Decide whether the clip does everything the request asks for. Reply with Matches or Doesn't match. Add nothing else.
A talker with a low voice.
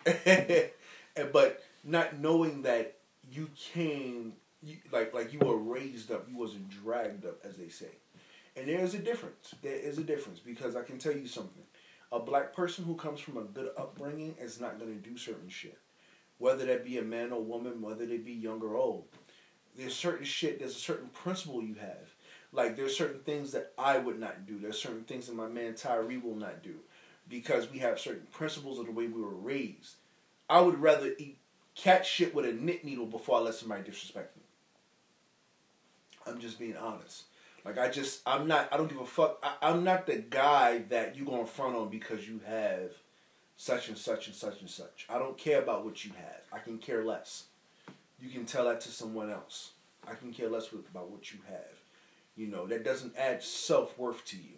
Matches